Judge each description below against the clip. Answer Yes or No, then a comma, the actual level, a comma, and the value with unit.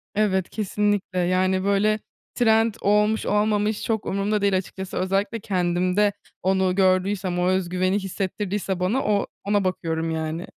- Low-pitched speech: No, high, 195 Hz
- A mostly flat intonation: Yes, narrow, 2.1 semitones